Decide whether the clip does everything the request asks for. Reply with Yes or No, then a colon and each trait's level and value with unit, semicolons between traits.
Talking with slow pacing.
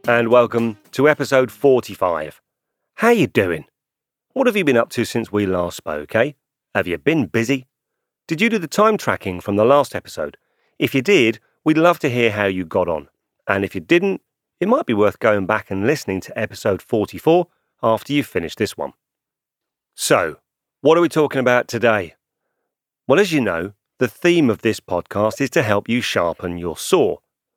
No: average, 190 wpm